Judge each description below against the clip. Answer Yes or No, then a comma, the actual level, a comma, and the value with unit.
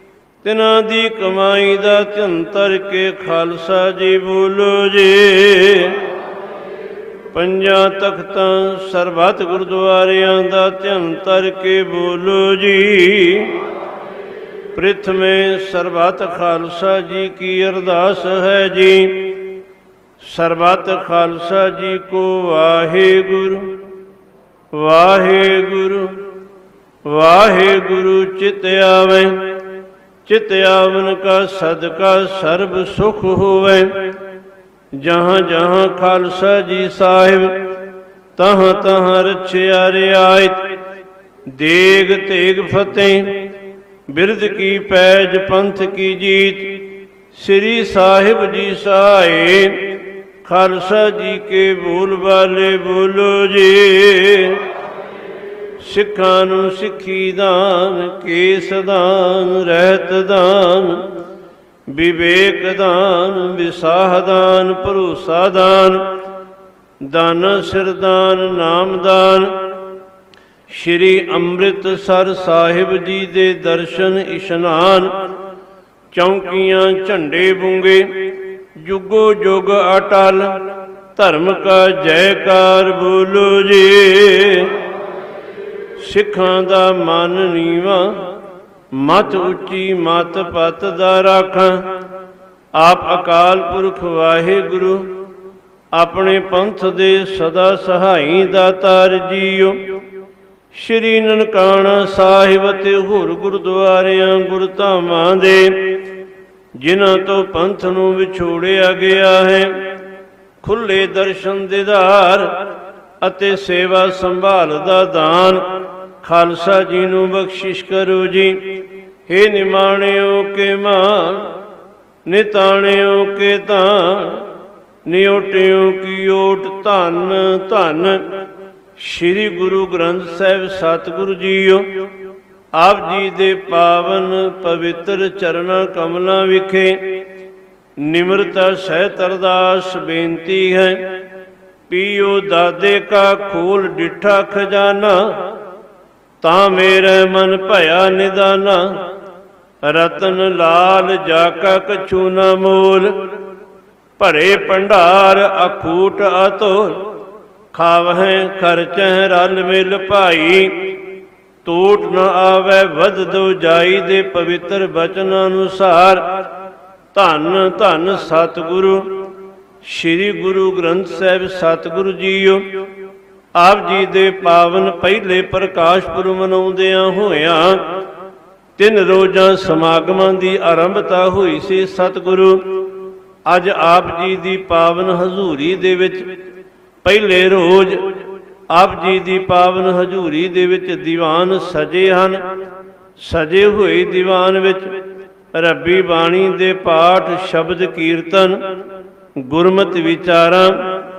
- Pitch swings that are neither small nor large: No, narrow, 0.7 semitones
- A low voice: No, high, 190 Hz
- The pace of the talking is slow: Yes, slow, 85 wpm